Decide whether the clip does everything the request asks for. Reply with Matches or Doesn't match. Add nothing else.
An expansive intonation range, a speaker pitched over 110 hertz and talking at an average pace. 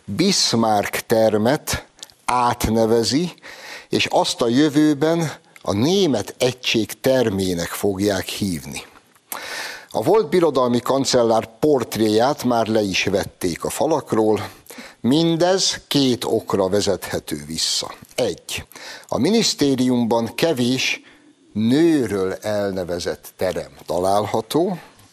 Doesn't match